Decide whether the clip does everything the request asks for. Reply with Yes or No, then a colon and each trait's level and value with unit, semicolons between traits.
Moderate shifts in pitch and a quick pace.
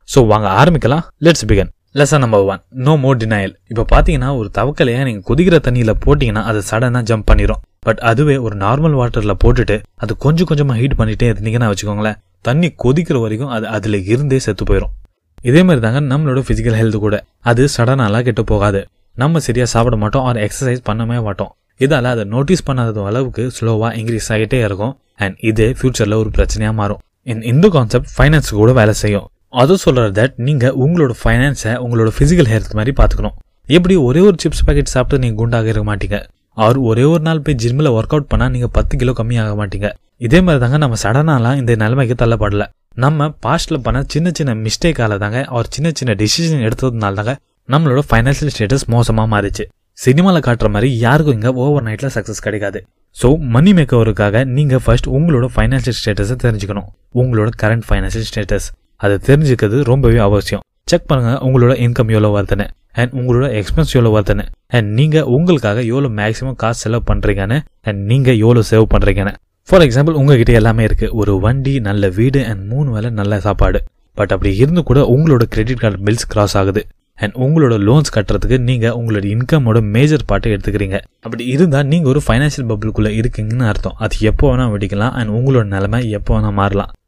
Yes: average, 4.2 semitones; fast, 160 wpm